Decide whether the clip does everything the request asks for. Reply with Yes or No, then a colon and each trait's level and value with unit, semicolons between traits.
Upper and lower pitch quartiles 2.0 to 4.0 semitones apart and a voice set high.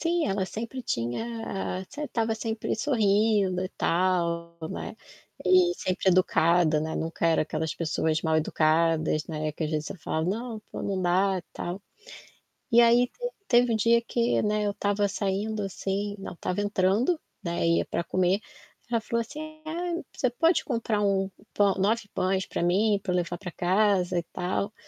No: average, 4.6 semitones; high, 195 Hz